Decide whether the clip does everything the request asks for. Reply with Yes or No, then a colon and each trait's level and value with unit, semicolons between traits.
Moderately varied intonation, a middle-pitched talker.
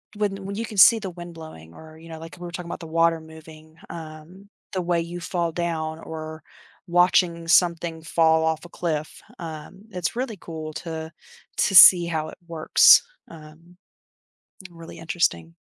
No: narrow, 1.8 semitones; medium, 165 Hz